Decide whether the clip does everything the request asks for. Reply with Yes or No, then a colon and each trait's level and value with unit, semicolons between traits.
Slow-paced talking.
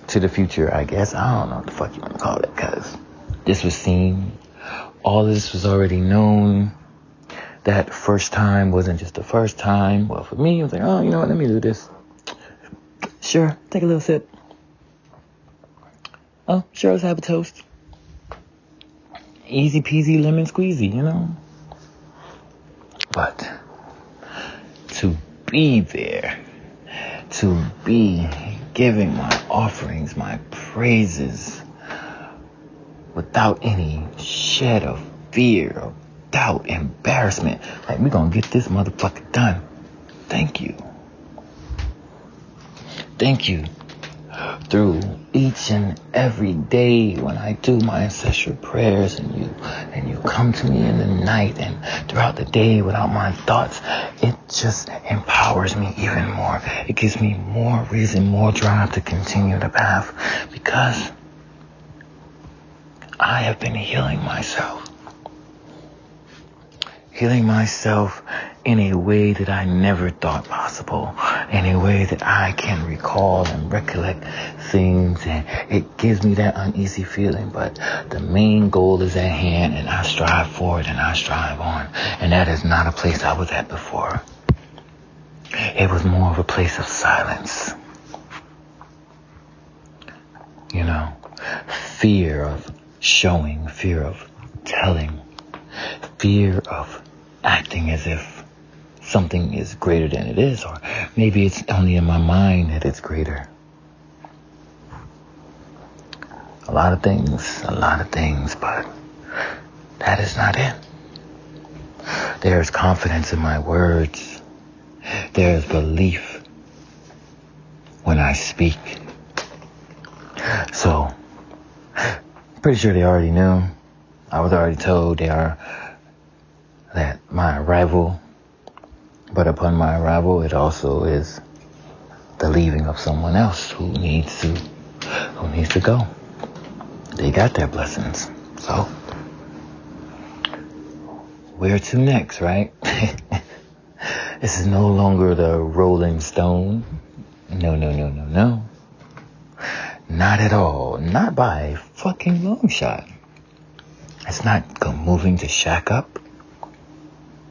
Yes: slow, 125 wpm